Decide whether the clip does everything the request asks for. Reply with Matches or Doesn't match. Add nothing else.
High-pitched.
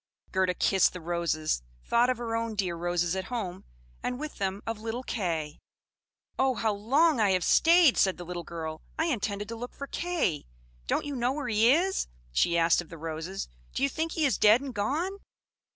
Matches